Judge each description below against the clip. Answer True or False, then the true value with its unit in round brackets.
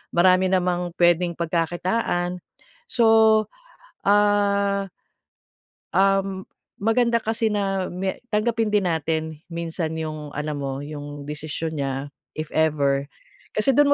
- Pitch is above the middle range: False (180 Hz)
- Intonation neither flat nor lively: True (4.6 semitones)